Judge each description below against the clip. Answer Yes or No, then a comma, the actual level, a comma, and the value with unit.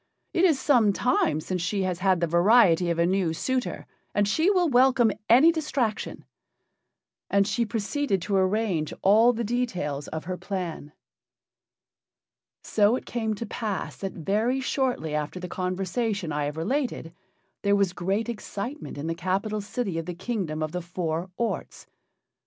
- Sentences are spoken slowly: No, average, 160 wpm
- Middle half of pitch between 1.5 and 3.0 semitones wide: No, average, 5.3 semitones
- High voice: Yes, high, 200 Hz